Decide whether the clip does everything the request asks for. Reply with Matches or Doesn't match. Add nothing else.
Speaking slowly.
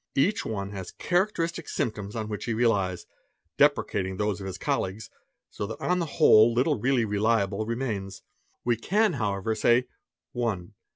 Doesn't match